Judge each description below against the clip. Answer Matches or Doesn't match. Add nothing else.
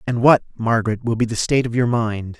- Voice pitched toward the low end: Matches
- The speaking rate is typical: Doesn't match